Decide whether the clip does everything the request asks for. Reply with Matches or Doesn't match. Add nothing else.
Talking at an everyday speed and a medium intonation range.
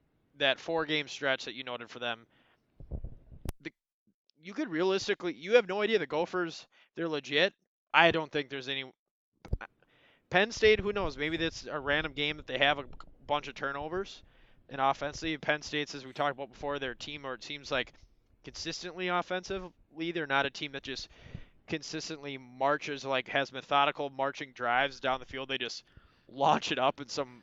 Matches